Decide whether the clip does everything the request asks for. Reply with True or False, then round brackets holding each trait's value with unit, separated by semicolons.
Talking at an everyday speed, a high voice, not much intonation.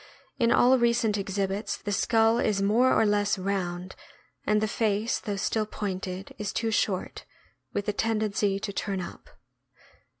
True (155 wpm; 205 Hz; 2.2 semitones)